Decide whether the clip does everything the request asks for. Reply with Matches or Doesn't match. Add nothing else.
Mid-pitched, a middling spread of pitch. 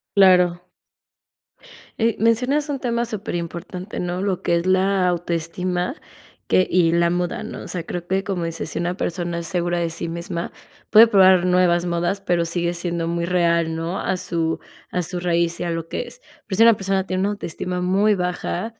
Doesn't match